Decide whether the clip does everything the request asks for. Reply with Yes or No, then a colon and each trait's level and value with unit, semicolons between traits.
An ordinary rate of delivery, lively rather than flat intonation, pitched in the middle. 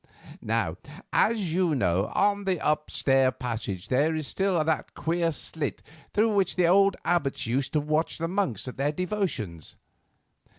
Yes: average, 155 wpm; wide, 5.8 semitones; medium, 160 Hz